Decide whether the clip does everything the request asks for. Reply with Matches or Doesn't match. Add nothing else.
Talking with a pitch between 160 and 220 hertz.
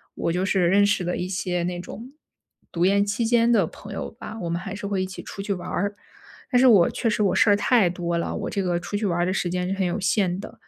Matches